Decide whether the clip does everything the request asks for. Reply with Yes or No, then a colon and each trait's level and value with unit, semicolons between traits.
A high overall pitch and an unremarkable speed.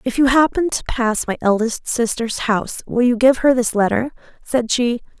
Yes: high, 240 Hz; average, 195 wpm